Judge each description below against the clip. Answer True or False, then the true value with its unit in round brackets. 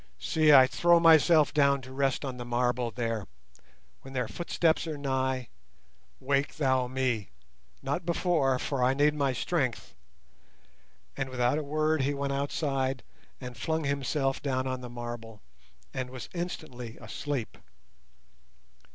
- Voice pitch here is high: False (135 Hz)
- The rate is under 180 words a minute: True (140 wpm)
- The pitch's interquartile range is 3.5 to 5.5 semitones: False (2.8 semitones)